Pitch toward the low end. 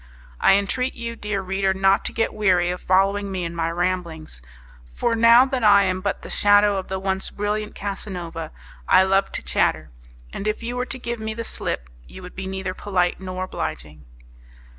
No: high, 195 Hz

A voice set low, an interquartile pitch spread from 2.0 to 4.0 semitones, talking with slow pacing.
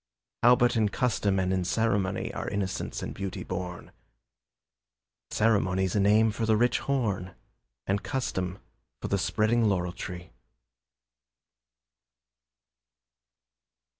Yes: low, 100 Hz; average, 3.2 semitones; slow, 110 wpm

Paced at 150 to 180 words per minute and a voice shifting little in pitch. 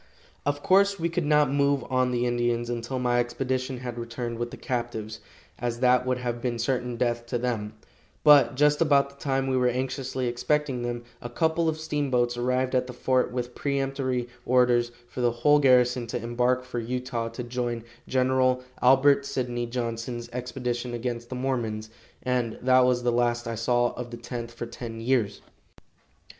Yes: average, 175 wpm; narrow, 1.6 semitones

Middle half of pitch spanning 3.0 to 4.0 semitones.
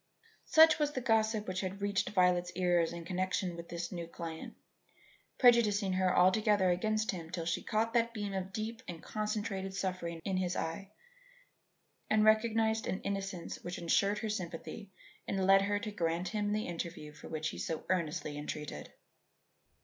Yes: average, 3.7 semitones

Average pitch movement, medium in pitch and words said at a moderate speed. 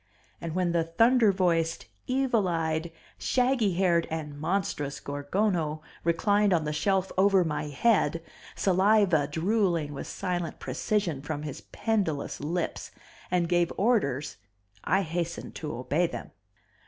No: average, 4.3 semitones; medium, 170 Hz; slow, 130 wpm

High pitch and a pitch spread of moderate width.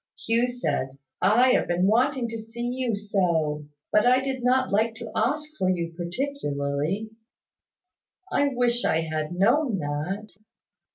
No: high, 215 Hz; wide, 6.4 semitones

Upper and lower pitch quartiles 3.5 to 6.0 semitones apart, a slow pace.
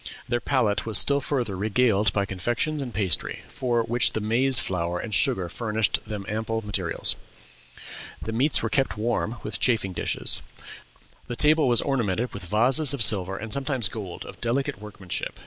No: average, 3.9 semitones; average, 165 wpm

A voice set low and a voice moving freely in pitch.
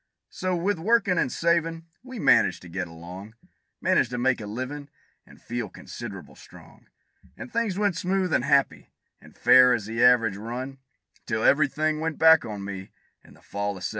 Yes: low, 130 Hz; wide, 7.3 semitones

